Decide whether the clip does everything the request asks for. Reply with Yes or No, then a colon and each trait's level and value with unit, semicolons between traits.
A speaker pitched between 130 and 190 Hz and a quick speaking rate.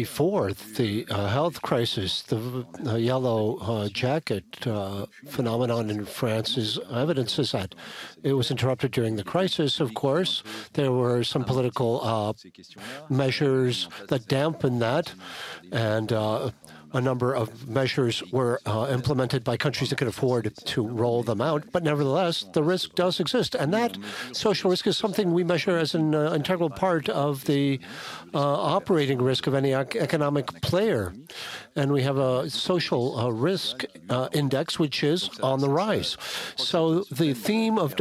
No: low, 135 Hz; average, 155 wpm